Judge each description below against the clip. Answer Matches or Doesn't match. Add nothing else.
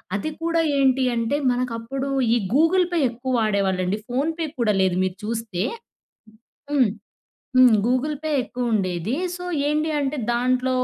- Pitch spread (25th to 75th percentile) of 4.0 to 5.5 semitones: Matches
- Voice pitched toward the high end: Matches